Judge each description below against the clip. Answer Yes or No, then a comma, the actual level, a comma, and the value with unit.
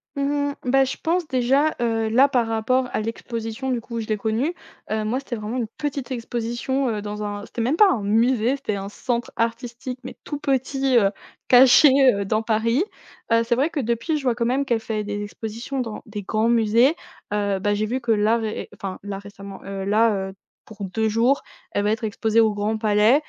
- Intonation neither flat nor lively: Yes, average, 3.3 semitones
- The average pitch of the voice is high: Yes, high, 230 Hz